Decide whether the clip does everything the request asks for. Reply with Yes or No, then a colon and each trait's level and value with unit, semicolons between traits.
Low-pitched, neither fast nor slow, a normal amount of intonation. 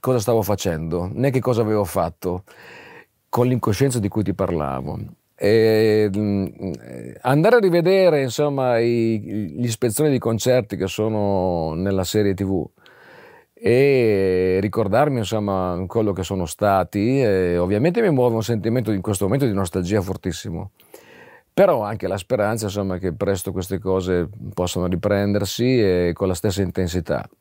Yes: low, 100 Hz; average, 140 wpm; average, 3.8 semitones